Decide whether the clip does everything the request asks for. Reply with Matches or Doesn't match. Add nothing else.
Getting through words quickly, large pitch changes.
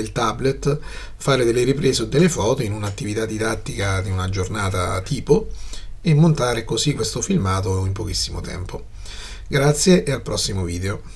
Doesn't match